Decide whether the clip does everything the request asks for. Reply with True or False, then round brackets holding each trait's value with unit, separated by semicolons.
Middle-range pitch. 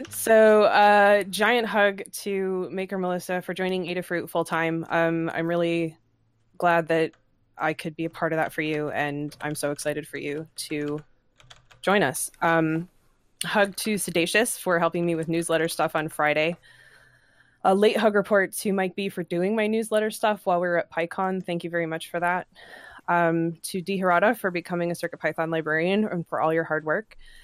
True (170 Hz)